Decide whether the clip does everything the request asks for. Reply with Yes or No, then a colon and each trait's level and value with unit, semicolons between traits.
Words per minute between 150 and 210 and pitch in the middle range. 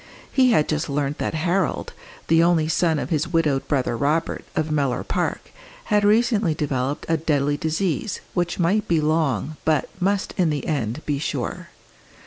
Yes: average, 165 wpm; medium, 155 Hz